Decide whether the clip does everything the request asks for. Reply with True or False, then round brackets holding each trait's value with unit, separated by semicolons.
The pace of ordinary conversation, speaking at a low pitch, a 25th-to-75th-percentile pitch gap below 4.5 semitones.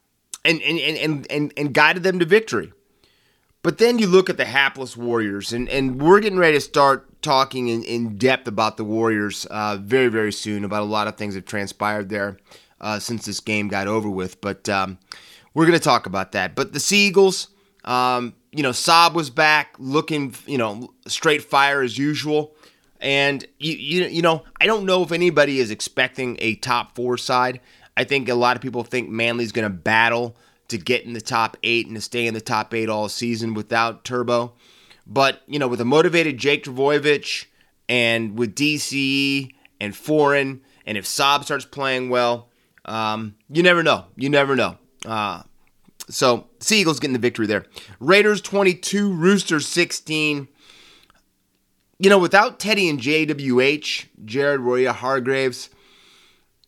False (175 wpm; 130 Hz; 4.9 semitones)